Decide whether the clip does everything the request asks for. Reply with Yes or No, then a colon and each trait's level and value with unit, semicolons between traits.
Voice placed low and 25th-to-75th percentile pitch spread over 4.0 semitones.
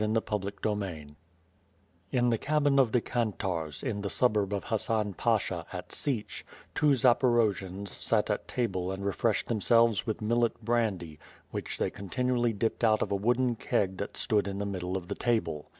No: low, 110 Hz; average, 3.5 semitones